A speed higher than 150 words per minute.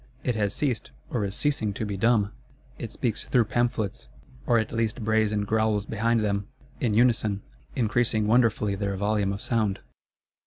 Yes: average, 160 wpm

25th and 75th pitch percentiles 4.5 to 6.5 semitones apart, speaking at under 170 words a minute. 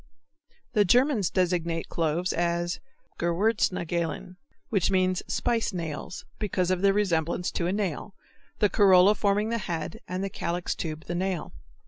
No: average, 2.7 semitones; average, 140 wpm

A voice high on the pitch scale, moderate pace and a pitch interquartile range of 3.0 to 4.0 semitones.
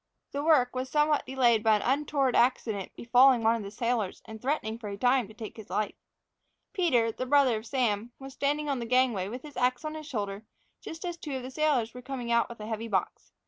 No: high, 245 Hz; fast, 230 wpm; average, 3.7 semitones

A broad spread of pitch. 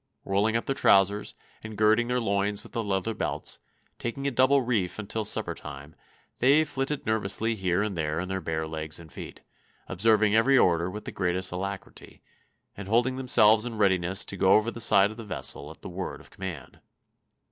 No: average, 3.6 semitones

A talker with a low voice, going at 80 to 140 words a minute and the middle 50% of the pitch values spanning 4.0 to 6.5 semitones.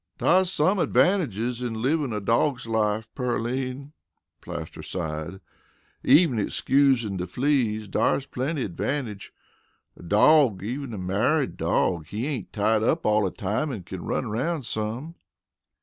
Yes: low, 115 Hz; slow, 135 wpm; average, 5.2 semitones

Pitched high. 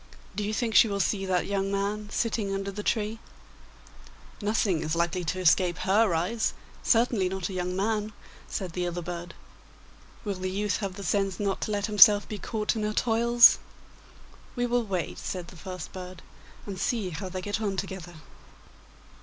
Yes: high, 195 Hz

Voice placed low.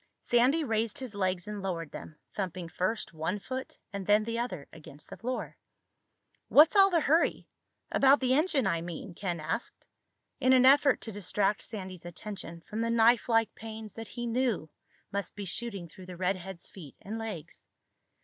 No: high, 210 Hz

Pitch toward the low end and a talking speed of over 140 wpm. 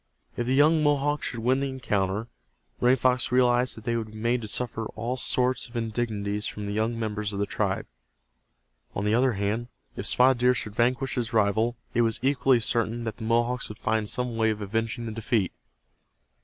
Yes: low, 115 Hz; average, 200 wpm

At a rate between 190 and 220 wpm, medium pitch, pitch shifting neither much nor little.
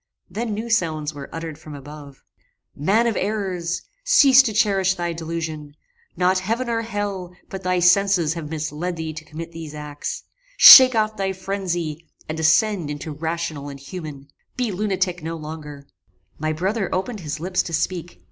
No: average, 165 wpm; medium, 170 Hz; average, 4.1 semitones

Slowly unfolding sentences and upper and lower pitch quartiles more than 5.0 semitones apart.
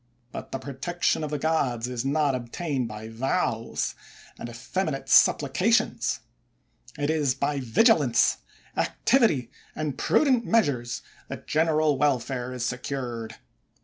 No: slow, 120 wpm; average, 4.2 semitones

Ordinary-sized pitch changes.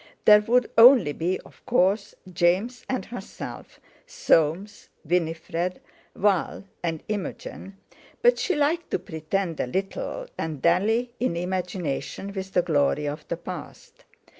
Yes: average, 4.9 semitones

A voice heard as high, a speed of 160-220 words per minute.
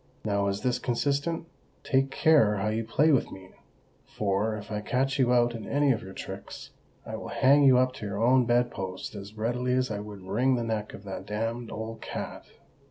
No: low, 115 Hz; average, 195 wpm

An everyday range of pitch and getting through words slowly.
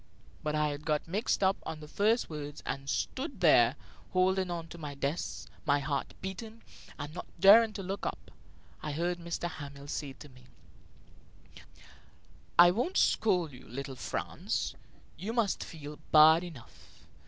No: average, 4.7 semitones; average, 155 wpm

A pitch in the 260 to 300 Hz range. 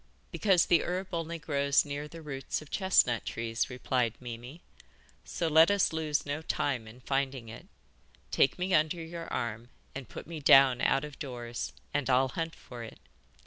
No: medium, 140 Hz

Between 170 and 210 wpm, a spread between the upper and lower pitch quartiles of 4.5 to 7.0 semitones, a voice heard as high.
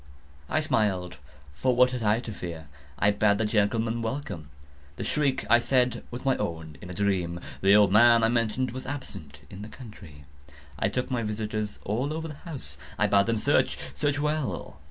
No: average, 180 wpm; average, 4.8 semitones; low, 110 Hz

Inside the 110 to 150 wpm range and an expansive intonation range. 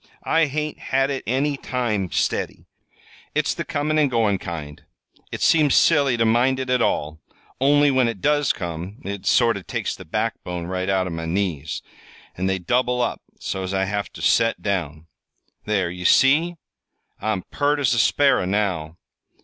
No: average, 175 wpm; wide, 6.5 semitones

